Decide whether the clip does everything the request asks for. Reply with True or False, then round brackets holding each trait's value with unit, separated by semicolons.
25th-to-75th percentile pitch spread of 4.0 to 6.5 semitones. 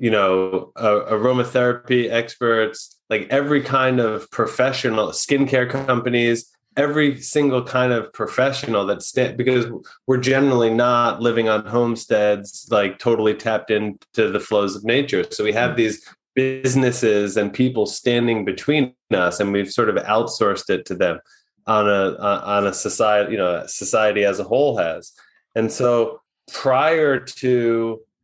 False (3.2 semitones)